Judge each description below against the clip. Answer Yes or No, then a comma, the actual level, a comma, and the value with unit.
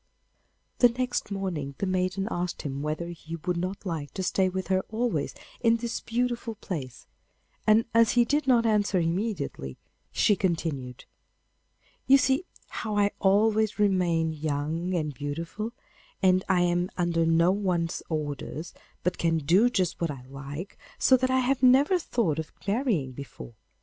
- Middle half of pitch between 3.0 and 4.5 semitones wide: No, wide, 5.4 semitones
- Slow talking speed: No, average, 155 wpm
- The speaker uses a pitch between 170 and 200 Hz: Yes, medium, 185 Hz